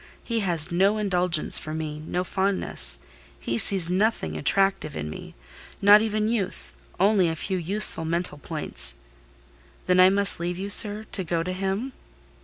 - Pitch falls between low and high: Yes, medium, 180 Hz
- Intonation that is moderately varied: Yes, average, 4.3 semitones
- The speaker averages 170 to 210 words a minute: No, average, 145 wpm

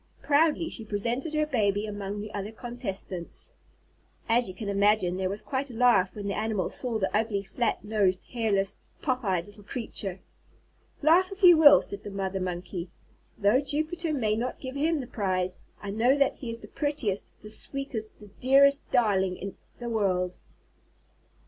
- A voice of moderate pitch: No, high, 215 Hz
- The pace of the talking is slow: No, average, 175 wpm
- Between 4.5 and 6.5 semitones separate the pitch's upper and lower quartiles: Yes, average, 4.9 semitones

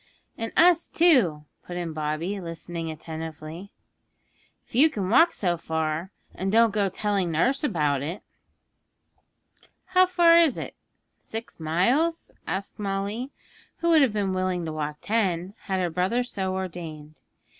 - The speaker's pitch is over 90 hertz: Yes, high, 190 Hz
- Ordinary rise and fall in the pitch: No, wide, 6.0 semitones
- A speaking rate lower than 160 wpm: Yes, average, 145 wpm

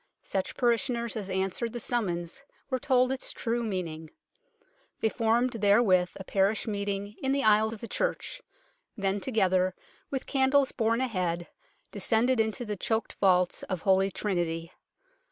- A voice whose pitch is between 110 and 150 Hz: No, high, 210 Hz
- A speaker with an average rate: Yes, average, 150 wpm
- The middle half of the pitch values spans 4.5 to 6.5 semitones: No, average, 4.0 semitones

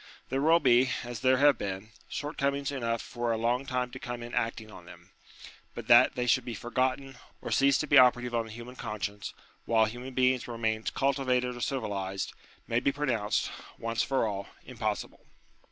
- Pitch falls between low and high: No, low, 120 Hz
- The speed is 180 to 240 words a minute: Yes, average, 185 wpm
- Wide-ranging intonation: No, average, 2.8 semitones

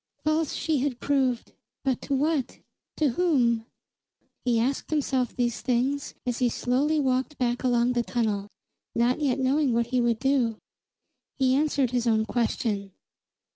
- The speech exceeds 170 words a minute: No, average, 150 wpm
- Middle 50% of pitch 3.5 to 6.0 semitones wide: No, average, 2.9 semitones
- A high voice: Yes, very high, 250 Hz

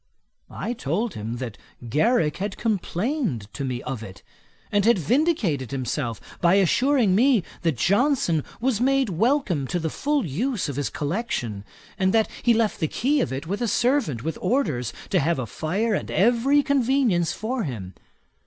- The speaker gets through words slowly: No, average, 170 wpm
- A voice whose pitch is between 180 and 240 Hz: Yes, high, 190 Hz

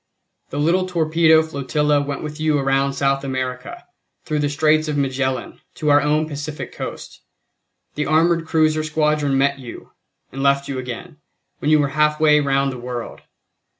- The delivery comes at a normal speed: Yes, average, 165 wpm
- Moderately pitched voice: Yes, medium, 145 Hz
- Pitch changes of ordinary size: No, narrow, 2.1 semitones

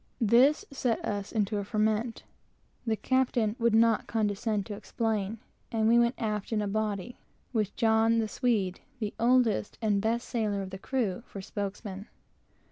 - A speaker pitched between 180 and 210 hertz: No, high, 220 Hz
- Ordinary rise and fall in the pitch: No, narrow, 2.2 semitones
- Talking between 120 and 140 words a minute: No, average, 155 wpm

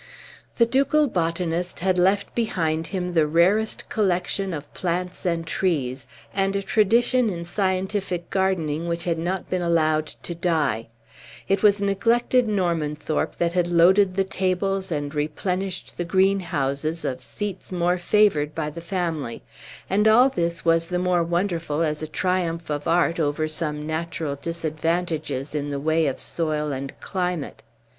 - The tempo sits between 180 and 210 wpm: No, average, 150 wpm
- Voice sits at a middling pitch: Yes, medium, 170 Hz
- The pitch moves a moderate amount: Yes, average, 3.3 semitones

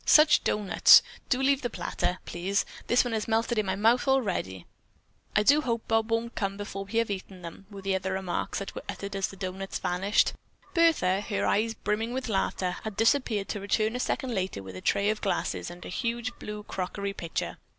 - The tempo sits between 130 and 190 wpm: No, fast, 205 wpm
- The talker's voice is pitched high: Yes, high, 205 Hz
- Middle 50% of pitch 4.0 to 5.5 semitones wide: No, average, 3.2 semitones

